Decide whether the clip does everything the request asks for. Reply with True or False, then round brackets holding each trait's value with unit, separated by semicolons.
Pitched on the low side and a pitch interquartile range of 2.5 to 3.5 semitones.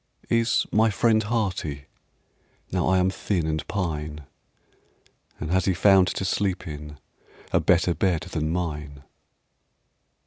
False (90 Hz; 4.1 semitones)